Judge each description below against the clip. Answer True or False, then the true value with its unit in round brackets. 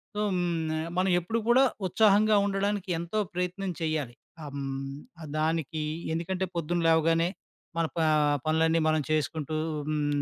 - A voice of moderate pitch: True (165 Hz)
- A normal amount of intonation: True (3.4 semitones)